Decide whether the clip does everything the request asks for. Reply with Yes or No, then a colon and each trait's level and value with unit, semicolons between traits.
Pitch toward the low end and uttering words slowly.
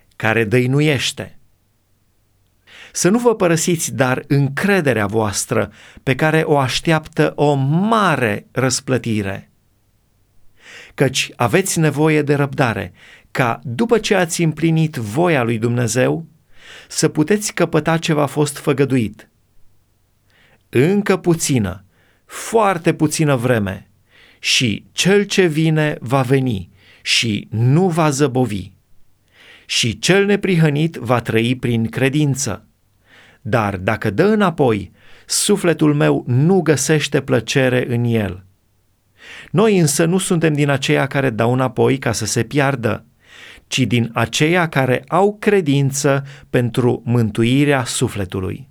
Yes: low, 130 Hz; slow, 110 wpm